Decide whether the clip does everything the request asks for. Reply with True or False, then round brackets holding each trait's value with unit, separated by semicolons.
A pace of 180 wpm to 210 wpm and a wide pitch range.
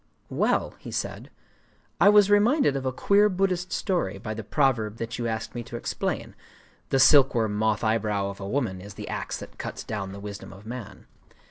True (190 wpm; 5.8 semitones)